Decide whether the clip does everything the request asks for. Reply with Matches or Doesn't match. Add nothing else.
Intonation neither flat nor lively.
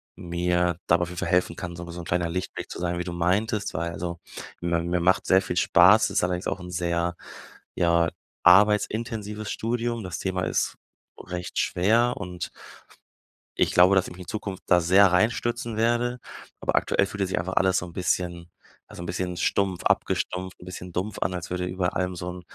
Doesn't match